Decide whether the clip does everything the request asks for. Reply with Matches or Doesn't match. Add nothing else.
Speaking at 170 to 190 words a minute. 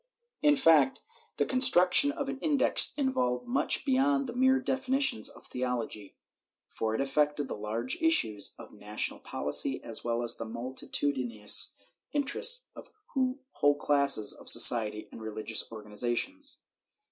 Doesn't match